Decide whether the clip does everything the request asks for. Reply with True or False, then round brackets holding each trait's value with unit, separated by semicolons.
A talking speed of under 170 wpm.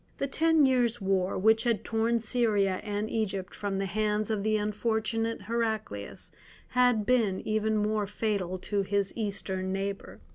True (150 wpm)